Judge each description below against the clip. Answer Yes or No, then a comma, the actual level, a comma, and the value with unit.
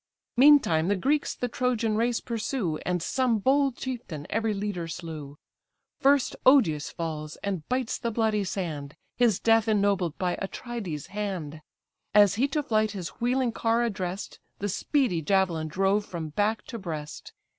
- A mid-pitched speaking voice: No, high, 205 Hz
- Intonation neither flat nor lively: No, wide, 5.7 semitones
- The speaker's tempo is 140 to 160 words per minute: Yes, average, 150 wpm